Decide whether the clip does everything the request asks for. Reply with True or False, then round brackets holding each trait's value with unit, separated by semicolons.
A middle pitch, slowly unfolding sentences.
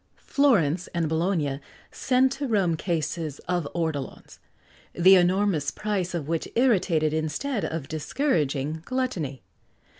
True (170 Hz; 115 wpm)